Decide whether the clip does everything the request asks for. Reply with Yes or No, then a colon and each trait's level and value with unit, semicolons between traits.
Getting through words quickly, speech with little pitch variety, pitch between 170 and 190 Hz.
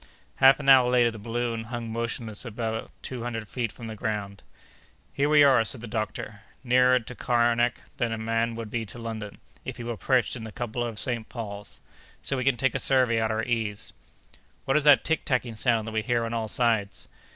No: fast, 215 wpm; narrow, 1.9 semitones; low, 115 Hz